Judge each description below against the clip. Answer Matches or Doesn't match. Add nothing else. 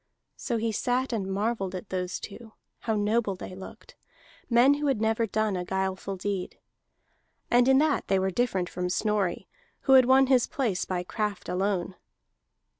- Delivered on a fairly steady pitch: Doesn't match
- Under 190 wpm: Matches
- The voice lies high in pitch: Matches